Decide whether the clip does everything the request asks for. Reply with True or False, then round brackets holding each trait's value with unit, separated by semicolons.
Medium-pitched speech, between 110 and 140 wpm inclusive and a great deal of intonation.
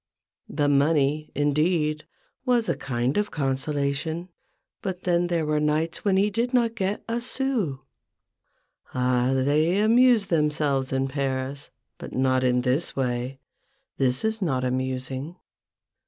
True (150 Hz; 135 wpm; 5.9 semitones)